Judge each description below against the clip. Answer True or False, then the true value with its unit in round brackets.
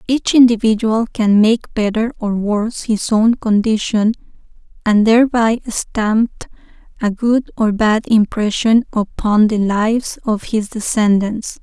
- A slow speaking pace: True (125 wpm)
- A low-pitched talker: False (220 Hz)